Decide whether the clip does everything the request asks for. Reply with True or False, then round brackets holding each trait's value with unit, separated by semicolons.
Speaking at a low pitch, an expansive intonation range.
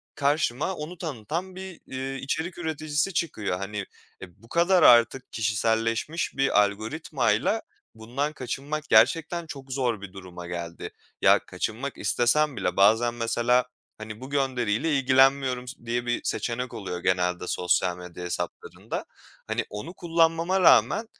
True (125 Hz; 6.0 semitones)